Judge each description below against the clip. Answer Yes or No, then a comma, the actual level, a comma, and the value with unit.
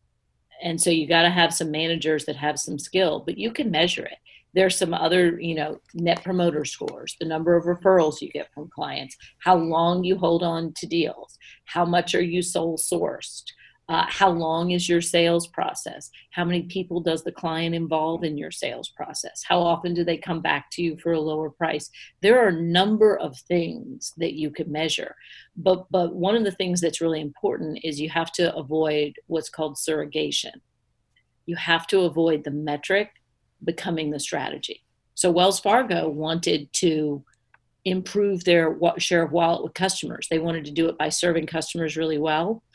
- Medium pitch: Yes, medium, 165 Hz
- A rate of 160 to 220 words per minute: Yes, average, 190 wpm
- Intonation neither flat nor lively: No, narrow, 1.9 semitones